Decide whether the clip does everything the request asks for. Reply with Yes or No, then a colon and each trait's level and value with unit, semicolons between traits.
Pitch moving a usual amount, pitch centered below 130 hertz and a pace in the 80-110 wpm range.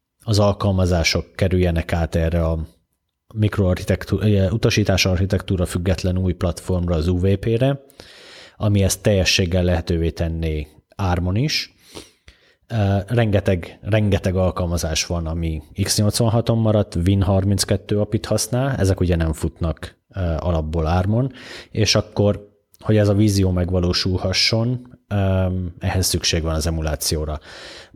Yes: average, 3.0 semitones; very low, 95 Hz; slow, 105 wpm